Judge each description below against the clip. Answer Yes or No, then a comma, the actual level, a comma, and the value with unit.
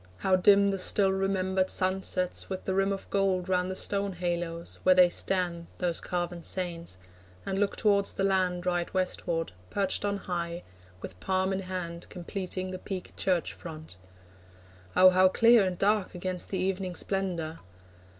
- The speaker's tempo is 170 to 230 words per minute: No, average, 160 wpm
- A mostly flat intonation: Yes, narrow, 1.6 semitones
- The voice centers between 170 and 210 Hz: Yes, medium, 185 Hz